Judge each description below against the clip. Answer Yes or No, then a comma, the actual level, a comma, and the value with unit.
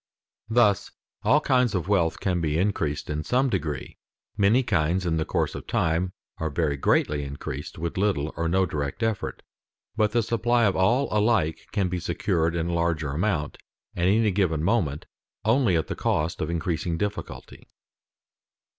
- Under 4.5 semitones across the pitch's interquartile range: No, average, 4.8 semitones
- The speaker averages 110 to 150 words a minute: No, average, 165 wpm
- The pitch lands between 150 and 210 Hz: No, very low, 90 Hz